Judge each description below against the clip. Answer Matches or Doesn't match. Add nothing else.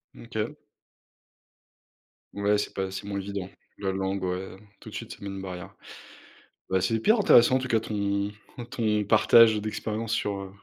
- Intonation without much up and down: Matches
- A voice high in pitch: Doesn't match